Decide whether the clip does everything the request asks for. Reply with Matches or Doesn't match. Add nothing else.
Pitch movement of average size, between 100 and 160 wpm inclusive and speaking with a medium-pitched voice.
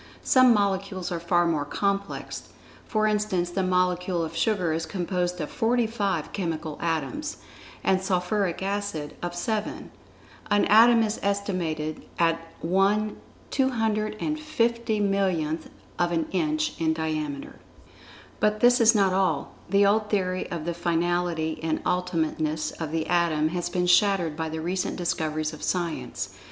Matches